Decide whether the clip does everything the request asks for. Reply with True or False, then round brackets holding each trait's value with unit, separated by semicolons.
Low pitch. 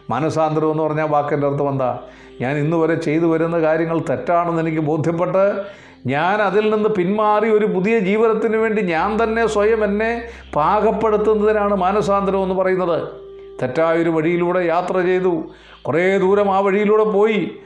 False (185 Hz)